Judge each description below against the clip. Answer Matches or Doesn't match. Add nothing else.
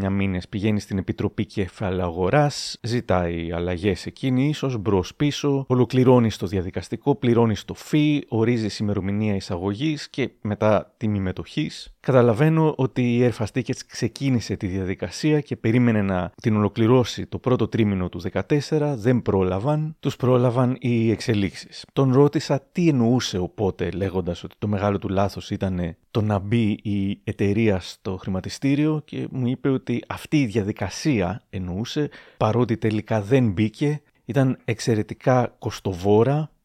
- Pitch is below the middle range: Matches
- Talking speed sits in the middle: Matches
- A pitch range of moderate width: Matches